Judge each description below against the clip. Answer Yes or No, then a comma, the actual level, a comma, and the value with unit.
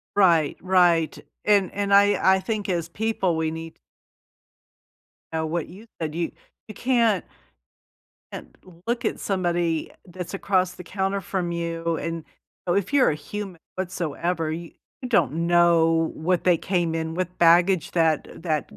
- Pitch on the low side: No, medium, 175 Hz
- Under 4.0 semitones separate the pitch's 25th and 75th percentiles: Yes, average, 2.8 semitones